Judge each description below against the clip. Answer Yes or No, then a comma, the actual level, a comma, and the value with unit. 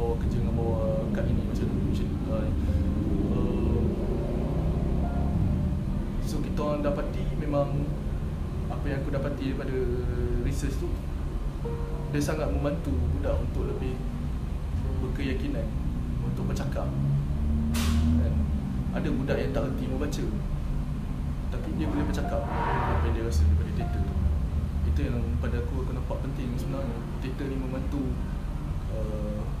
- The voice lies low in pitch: Yes, very low, 75 Hz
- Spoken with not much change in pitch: Yes, narrow, 2.0 semitones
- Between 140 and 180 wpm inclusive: No, average, 125 wpm